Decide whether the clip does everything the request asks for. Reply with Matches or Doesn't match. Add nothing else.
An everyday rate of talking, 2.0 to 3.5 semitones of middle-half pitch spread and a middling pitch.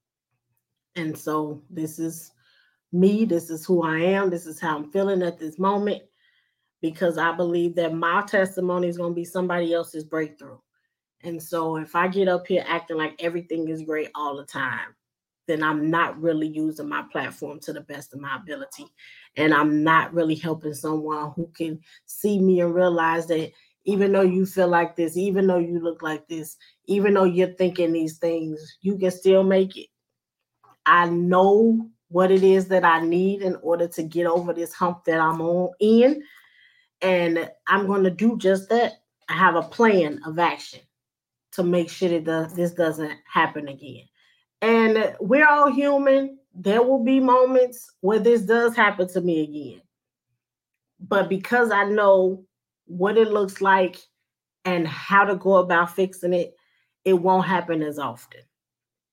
Matches